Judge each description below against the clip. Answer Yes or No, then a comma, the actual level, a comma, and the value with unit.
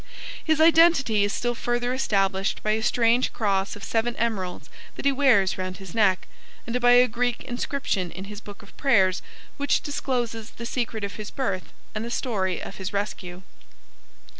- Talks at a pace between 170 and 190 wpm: Yes, average, 175 wpm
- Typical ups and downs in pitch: Yes, average, 3.9 semitones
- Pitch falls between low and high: No, high, 225 Hz